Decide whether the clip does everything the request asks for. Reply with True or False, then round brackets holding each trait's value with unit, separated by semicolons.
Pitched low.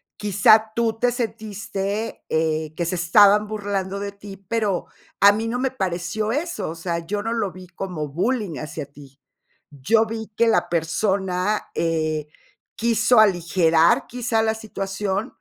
False (200 Hz)